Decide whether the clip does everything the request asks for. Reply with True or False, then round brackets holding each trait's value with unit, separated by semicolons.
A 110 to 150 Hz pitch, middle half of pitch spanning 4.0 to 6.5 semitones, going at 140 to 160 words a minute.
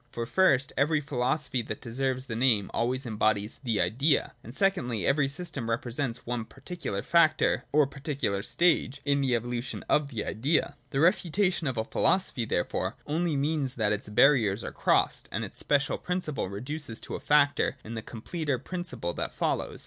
False (135 Hz; 4.7 semitones; 170 wpm)